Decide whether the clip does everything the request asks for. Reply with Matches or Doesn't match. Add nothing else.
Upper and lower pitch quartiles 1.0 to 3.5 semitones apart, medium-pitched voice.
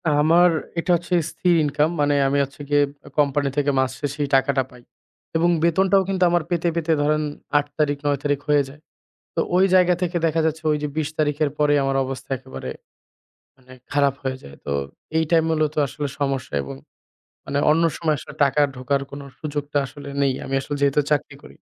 Matches